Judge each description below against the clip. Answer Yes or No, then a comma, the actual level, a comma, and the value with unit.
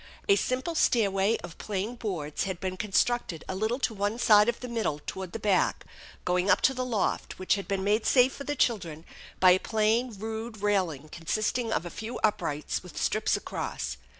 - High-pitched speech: Yes, high, 210 Hz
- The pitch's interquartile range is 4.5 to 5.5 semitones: No, average, 4.1 semitones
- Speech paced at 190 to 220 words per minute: Yes, average, 195 wpm